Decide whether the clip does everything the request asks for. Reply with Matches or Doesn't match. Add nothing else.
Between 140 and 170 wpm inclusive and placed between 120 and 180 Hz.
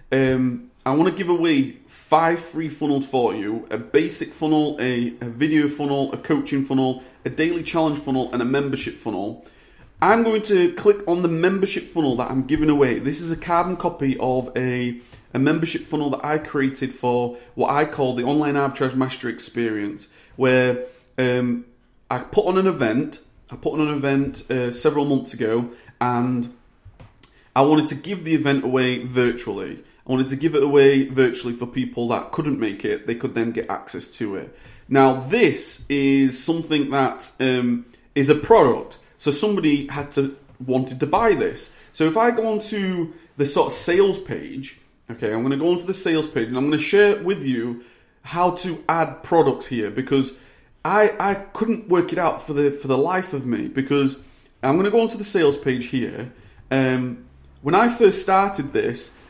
Doesn't match